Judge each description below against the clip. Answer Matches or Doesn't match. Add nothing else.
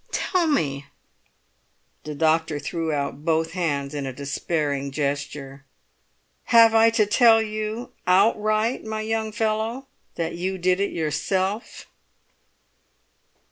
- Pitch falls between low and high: Matches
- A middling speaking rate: Doesn't match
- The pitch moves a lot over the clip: Matches